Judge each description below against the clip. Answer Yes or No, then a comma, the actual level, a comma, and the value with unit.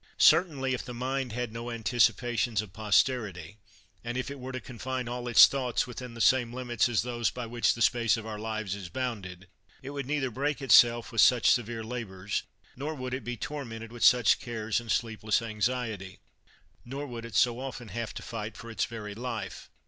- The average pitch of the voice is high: No, low, 120 Hz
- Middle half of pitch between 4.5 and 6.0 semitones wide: No, narrow, 2.4 semitones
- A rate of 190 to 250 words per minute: Yes, average, 195 wpm